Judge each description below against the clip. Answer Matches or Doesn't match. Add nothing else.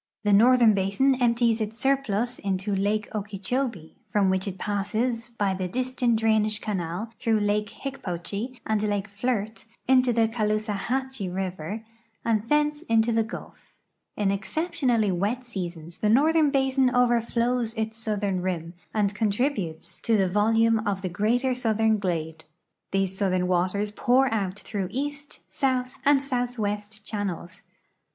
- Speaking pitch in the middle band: Doesn't match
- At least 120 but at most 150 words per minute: Matches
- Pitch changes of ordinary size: Matches